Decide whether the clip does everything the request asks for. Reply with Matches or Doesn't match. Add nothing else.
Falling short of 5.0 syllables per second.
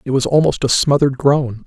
Doesn't match